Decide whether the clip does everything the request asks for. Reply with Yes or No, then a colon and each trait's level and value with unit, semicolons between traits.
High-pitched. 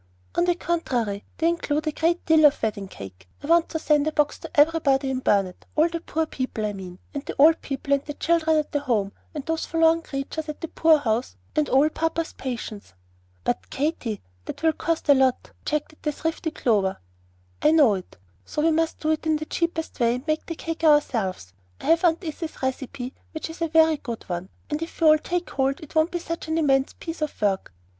Yes: very high, 300 Hz